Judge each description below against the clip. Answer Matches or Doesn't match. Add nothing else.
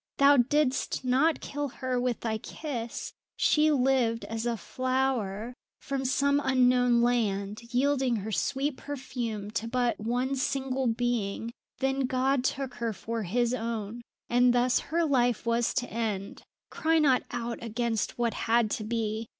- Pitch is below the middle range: Doesn't match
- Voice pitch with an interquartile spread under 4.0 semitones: Matches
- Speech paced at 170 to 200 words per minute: Doesn't match